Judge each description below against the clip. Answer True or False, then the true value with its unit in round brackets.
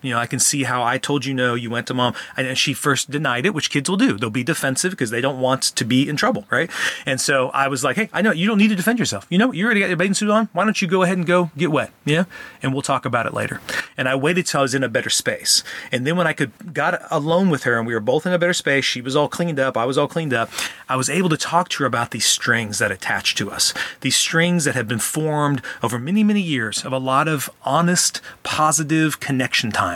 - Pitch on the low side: False (145 Hz)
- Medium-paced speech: False (285 wpm)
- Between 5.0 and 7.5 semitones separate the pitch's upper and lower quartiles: True (5.3 semitones)